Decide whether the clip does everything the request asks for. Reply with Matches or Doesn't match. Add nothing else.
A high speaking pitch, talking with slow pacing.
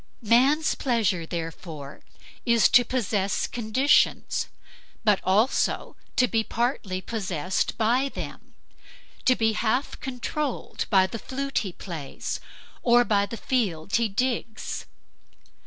Matches